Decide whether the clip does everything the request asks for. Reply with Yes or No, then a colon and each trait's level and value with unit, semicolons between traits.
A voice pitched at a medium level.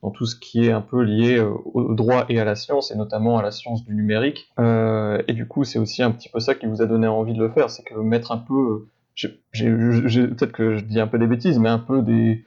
No: low, 115 Hz